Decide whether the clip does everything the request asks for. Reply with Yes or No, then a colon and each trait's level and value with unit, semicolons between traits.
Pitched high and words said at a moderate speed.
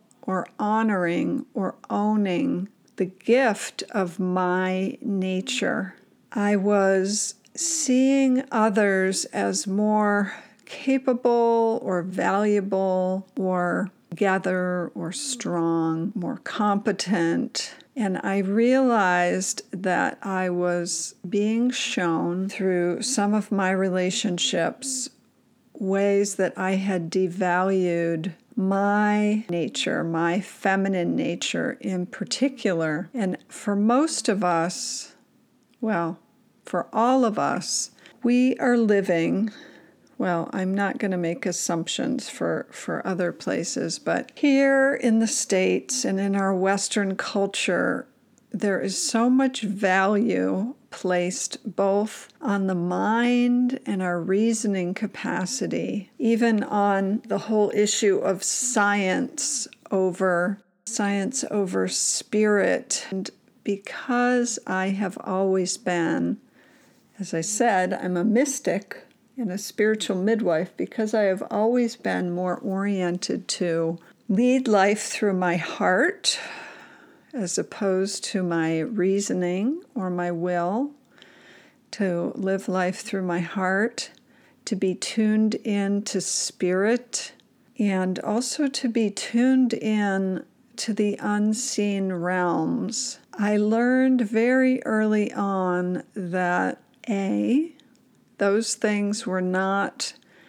No: high, 205 Hz; slow, 105 wpm